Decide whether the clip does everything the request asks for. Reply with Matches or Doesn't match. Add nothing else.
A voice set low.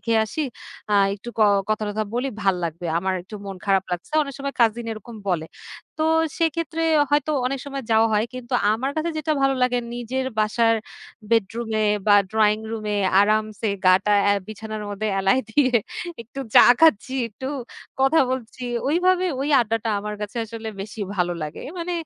Doesn't match